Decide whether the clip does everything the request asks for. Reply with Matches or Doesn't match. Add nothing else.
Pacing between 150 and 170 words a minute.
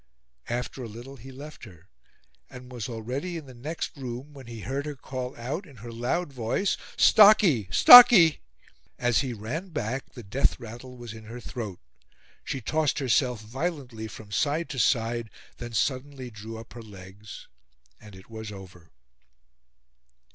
Matches